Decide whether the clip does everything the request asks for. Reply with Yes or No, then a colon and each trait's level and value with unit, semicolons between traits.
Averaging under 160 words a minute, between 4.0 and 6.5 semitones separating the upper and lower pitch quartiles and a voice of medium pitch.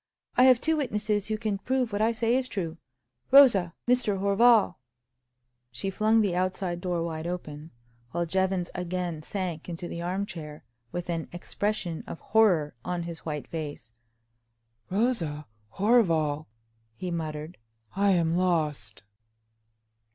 Yes: slow, 135 wpm; average, 4.4 semitones; medium, 180 Hz